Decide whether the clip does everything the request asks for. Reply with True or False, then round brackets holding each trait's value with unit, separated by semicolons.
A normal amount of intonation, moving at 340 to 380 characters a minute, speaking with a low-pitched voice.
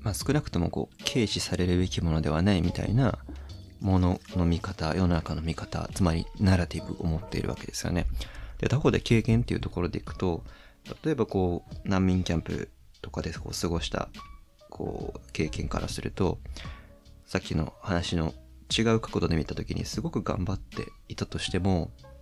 True (4.2 semitones; 355 characters per minute; 90 Hz)